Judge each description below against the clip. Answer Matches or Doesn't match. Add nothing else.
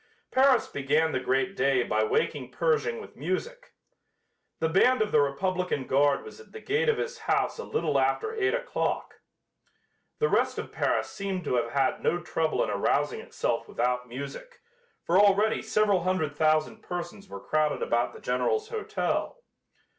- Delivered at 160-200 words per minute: Matches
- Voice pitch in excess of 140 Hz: Matches